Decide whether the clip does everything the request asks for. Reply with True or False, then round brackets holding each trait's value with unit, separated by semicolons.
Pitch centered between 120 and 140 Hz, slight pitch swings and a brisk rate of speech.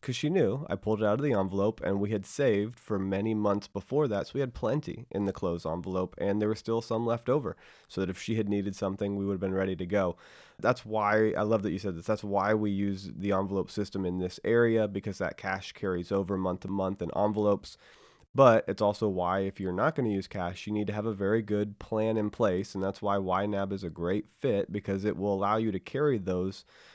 False (100 Hz; 2.0 semitones; 250 wpm)